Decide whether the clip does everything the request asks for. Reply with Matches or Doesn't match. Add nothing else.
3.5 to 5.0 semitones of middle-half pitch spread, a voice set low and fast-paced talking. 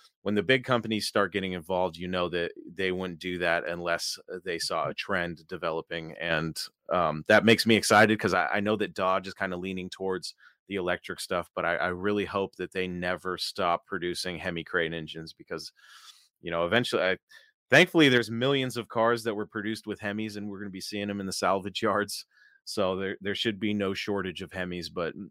Doesn't match